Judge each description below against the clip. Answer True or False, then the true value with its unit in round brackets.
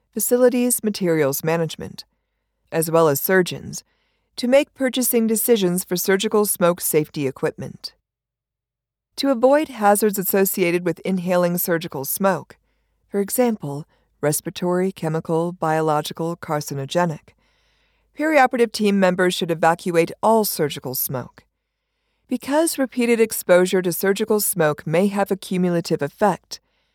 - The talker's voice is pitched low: False (185 Hz)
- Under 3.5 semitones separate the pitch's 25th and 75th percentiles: False (5.4 semitones)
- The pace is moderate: False (110 wpm)